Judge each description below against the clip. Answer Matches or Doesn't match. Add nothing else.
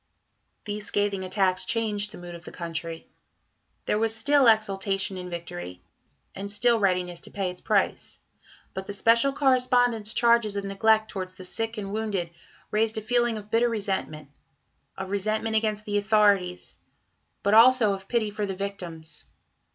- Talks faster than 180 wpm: Doesn't match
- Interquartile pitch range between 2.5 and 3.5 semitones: Matches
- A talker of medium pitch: Doesn't match